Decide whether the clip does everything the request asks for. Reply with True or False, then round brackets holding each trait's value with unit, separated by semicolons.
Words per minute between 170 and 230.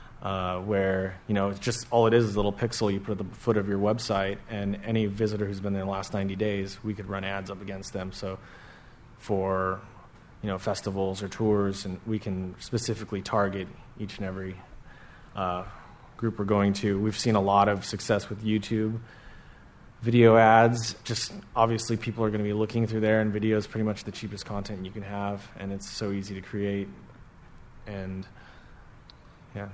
True (200 wpm)